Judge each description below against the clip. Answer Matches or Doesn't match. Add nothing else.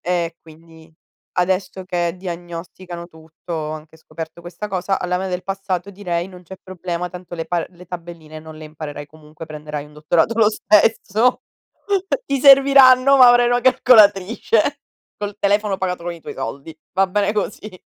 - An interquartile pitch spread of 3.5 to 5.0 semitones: Matches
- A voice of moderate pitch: Matches